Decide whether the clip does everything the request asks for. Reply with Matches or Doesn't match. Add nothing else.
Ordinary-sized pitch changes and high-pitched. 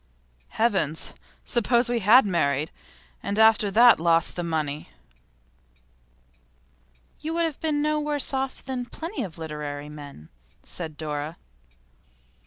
Doesn't match